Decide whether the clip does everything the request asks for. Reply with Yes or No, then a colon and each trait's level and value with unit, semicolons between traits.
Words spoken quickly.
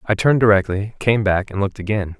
Yes: fast, 220 wpm